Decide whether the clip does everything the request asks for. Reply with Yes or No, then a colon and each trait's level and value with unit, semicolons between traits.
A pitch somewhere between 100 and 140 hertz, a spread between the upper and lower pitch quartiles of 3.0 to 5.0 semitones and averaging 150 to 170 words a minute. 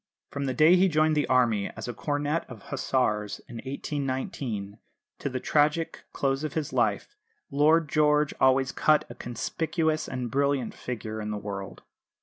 Yes: low, 135 Hz; average, 4.0 semitones; average, 160 wpm